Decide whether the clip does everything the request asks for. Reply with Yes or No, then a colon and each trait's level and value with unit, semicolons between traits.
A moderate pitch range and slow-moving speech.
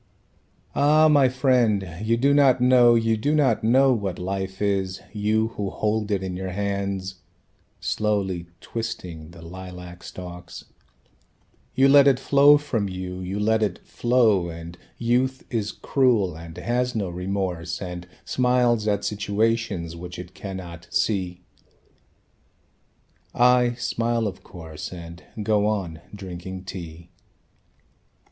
Yes: average, 4.7 semitones; slow, 130 wpm